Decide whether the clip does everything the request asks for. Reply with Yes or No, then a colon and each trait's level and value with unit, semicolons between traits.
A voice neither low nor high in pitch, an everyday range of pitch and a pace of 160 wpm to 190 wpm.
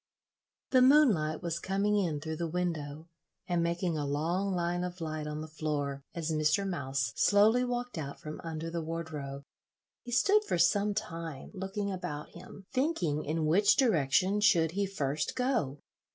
Yes: medium, 170 Hz; average, 4.6 semitones; average, 165 wpm